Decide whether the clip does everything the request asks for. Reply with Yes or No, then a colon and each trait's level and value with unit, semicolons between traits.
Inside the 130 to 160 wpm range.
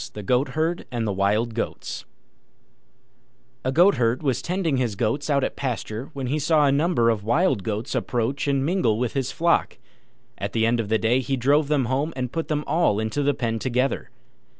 No: average, 195 wpm